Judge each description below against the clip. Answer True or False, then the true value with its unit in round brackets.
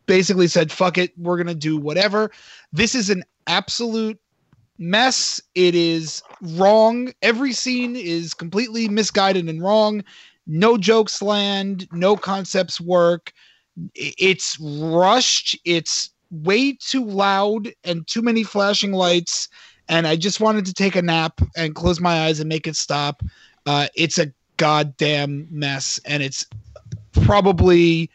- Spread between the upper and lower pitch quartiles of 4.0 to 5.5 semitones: True (4.7 semitones)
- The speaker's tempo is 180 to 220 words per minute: False (135 wpm)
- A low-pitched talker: False (180 Hz)